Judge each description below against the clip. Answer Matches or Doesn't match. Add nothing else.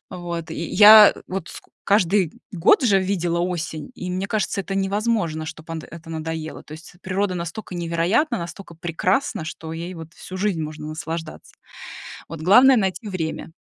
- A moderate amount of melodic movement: Matches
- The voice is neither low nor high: Matches